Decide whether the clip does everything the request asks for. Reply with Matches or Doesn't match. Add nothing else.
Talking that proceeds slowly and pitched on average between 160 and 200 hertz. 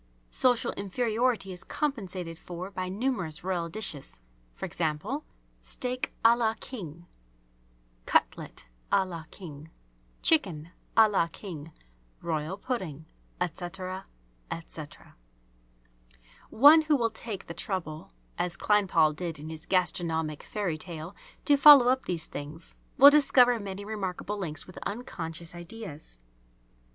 Matches